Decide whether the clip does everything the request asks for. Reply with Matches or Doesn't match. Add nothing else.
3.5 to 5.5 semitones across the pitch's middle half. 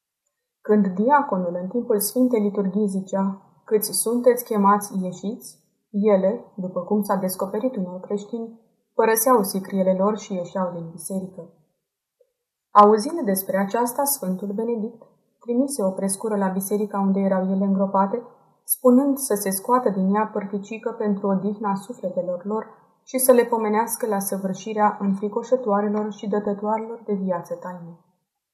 Doesn't match